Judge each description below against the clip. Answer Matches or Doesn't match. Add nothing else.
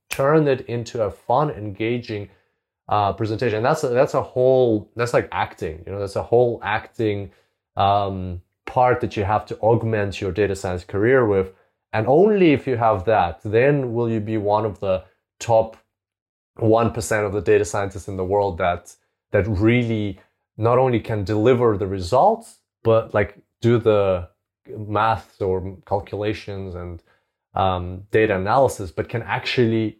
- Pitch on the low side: Matches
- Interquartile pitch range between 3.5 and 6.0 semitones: Doesn't match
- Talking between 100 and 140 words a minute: Doesn't match